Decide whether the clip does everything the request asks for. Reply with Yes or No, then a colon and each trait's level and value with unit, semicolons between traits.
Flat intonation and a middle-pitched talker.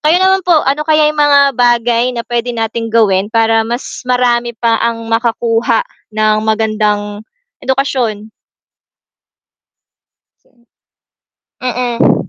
No: narrow, 2.3 semitones; high, 235 Hz